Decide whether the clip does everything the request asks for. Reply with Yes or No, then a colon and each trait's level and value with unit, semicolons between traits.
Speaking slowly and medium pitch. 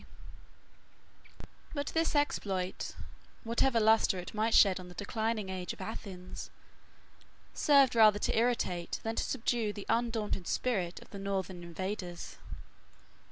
No: slow, 130 wpm; high, 210 Hz